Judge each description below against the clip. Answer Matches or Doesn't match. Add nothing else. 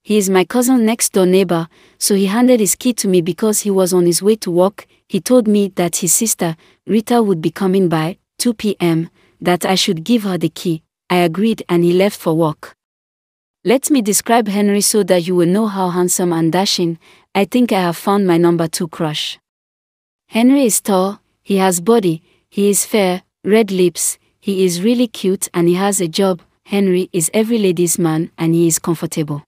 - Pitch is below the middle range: Doesn't match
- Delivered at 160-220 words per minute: Matches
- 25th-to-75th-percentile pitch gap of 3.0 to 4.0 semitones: Matches